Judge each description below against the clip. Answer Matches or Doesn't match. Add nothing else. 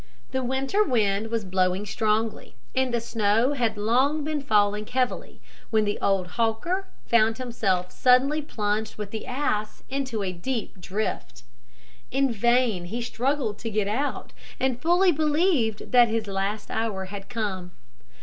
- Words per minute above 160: Doesn't match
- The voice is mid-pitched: Doesn't match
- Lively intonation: Doesn't match